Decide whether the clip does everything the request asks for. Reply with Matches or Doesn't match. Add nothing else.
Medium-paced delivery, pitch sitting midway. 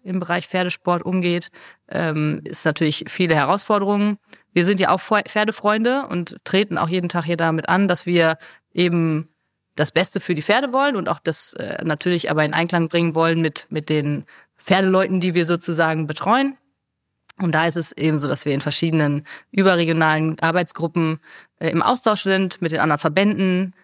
Matches